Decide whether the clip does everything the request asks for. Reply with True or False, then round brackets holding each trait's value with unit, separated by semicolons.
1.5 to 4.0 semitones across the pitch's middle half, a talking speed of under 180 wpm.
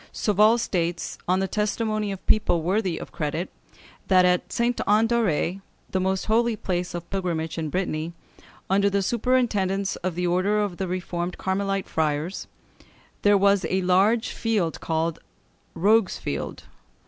True (3.1 semitones; 150 wpm)